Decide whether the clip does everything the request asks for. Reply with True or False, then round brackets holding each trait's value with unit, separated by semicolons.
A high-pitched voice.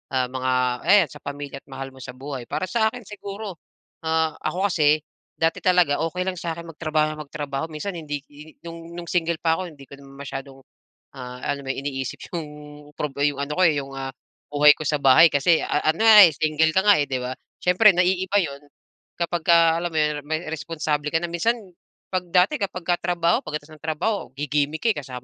False (155 Hz)